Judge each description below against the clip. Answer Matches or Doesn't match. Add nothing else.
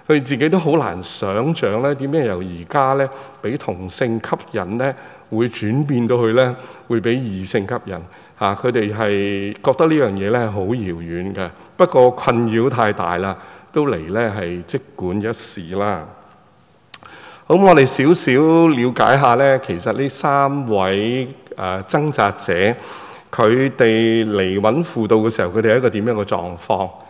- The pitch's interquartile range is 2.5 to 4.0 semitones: Doesn't match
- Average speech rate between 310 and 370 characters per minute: Doesn't match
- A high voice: Doesn't match